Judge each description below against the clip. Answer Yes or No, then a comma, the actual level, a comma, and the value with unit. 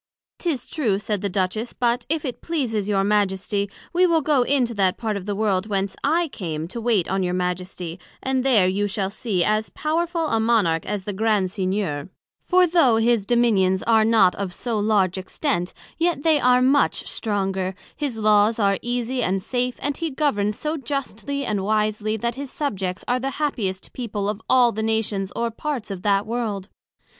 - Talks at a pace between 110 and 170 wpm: No, average, 190 wpm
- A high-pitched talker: Yes, high, 215 Hz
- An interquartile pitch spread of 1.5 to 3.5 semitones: No, average, 4.5 semitones